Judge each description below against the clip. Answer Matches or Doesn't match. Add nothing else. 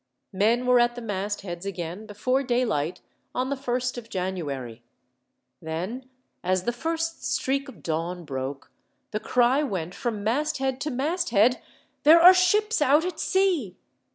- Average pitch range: Doesn't match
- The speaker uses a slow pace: Doesn't match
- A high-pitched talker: Matches